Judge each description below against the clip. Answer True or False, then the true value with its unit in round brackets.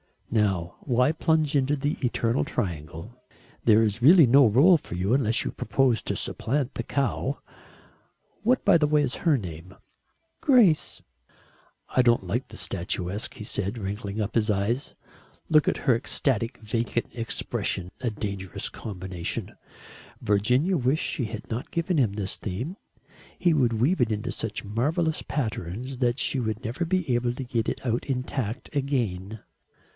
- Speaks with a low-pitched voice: True (120 Hz)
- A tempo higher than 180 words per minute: False (155 wpm)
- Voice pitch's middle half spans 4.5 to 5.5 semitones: True (5.1 semitones)